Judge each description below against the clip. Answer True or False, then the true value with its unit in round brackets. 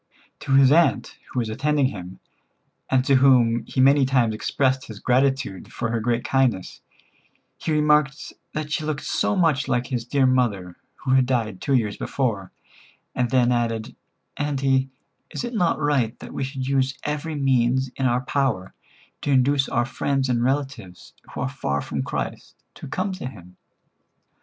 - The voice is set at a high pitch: False (130 Hz)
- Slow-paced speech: False (170 wpm)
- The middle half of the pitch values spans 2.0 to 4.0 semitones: True (2.8 semitones)